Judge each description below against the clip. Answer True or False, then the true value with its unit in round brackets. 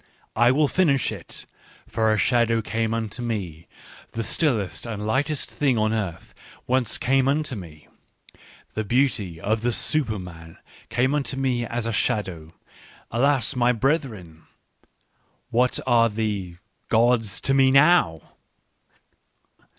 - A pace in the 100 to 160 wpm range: True (140 wpm)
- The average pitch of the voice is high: False (115 Hz)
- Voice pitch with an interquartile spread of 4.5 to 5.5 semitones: False (4.1 semitones)